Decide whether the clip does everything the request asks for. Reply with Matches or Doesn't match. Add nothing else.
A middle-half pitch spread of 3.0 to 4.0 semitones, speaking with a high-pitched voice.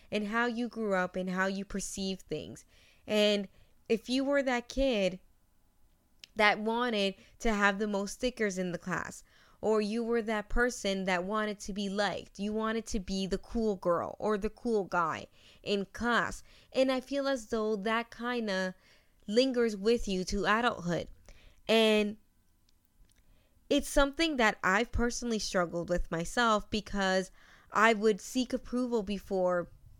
Matches